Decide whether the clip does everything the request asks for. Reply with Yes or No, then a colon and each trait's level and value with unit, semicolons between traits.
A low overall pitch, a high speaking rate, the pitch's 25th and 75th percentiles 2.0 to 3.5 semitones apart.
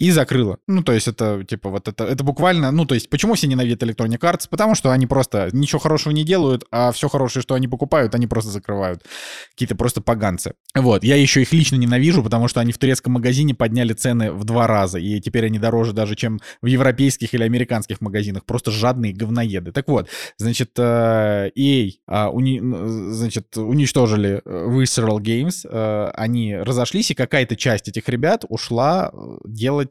Yes: low, 120 Hz; fast, 175 wpm; average, 3.1 semitones